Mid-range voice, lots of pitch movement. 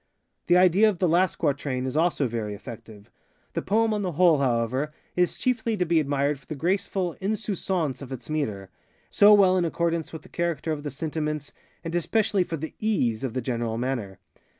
Yes: medium, 155 Hz; wide, 5.7 semitones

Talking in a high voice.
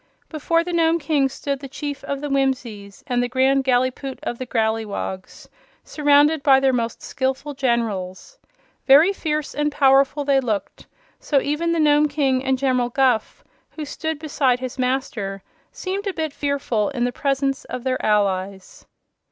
Yes: very high, 270 Hz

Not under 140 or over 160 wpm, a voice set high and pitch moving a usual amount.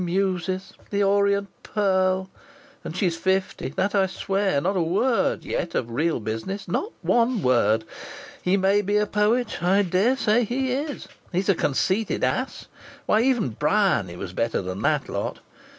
Yes: average, 155 wpm; high, 195 Hz; average, 3.3 semitones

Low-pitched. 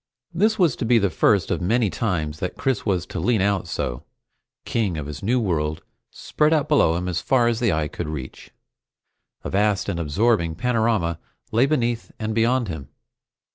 Yes: low, 100 Hz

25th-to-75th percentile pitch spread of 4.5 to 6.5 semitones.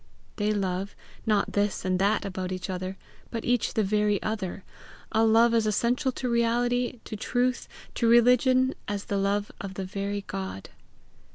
No: average, 3.2 semitones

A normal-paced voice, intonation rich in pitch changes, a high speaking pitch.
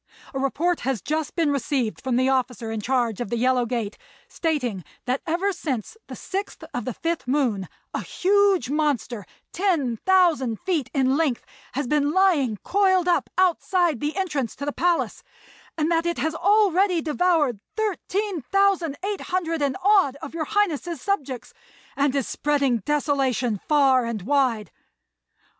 Yes: average, 150 wpm; wide, 5.7 semitones; very high, 295 Hz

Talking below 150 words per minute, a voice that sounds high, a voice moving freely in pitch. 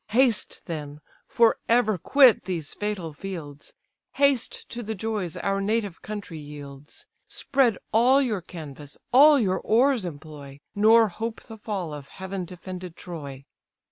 Yes: average, 140 wpm; high, 195 Hz; wide, 6.2 semitones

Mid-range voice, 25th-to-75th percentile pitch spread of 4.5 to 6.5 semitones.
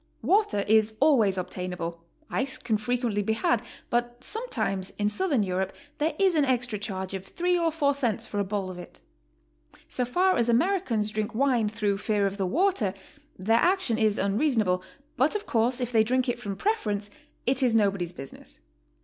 No: high, 225 Hz; wide, 5.4 semitones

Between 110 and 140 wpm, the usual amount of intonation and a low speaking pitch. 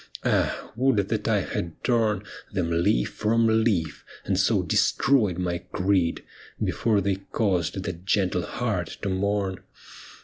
Yes: slow, 135 wpm; average, 3.4 semitones; very low, 95 Hz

